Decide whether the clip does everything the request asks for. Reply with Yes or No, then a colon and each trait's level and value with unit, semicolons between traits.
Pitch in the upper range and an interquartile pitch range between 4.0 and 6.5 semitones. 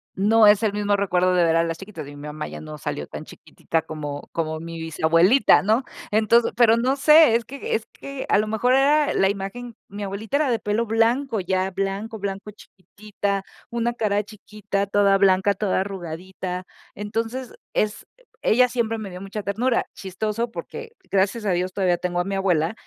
No: high, 205 Hz; average, 3.5 semitones